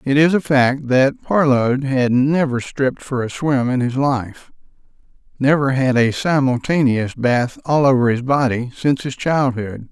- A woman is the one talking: No, male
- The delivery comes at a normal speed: Yes, average, 165 wpm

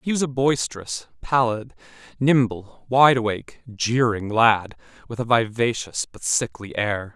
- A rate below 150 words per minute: Yes, slow, 135 wpm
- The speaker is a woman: No, male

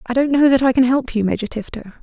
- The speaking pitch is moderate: No, high, 245 Hz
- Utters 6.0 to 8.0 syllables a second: Yes, 6.9 syllables/s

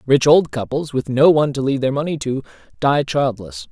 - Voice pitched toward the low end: Yes, low, 130 Hz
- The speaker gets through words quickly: Yes, fast, 210 wpm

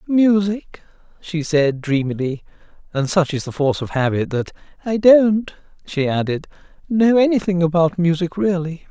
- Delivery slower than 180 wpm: Yes, average, 140 wpm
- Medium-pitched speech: Yes, medium, 170 Hz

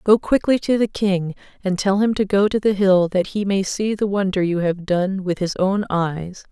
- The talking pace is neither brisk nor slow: No, fast, 240 wpm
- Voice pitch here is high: Yes, high, 195 Hz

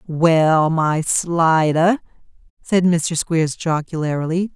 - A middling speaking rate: No, slow, 90 wpm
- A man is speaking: No, female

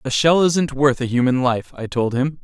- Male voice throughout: Yes, male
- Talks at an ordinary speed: No, fast, 245 wpm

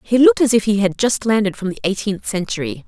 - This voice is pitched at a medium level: No, high, 205 Hz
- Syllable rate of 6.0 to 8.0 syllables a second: Yes, 6.3 syllables/s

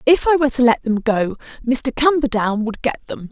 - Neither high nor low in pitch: No, very high, 250 Hz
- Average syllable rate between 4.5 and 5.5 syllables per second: Yes, 5.4 syllables/s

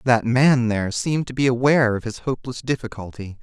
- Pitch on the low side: Yes, low, 120 Hz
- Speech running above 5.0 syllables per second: Yes, 6.1 syllables/s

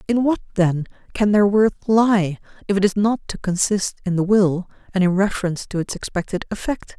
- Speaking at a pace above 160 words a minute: Yes, average, 195 wpm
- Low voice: No, high, 195 Hz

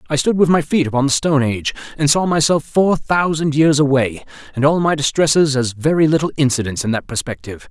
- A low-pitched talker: No, medium, 145 Hz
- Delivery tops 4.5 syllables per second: Yes, 6.1 syllables/s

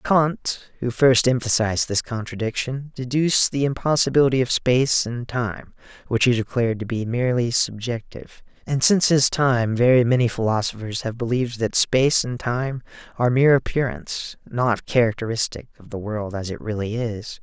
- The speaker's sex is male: Yes, male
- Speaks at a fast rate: No, average, 155 wpm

